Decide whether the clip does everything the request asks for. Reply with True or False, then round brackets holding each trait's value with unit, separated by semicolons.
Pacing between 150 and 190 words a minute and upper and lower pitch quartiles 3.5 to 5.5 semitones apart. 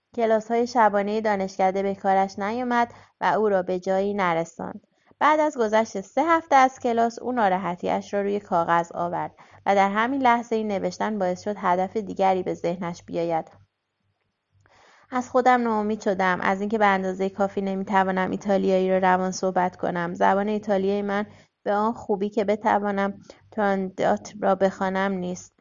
False (155 wpm; 2.7 semitones)